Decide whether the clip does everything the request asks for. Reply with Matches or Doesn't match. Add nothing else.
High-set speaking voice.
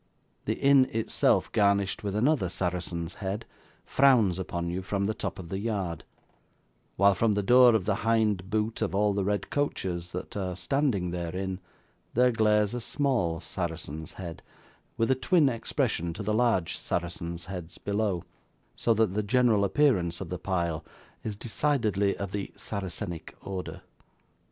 Doesn't match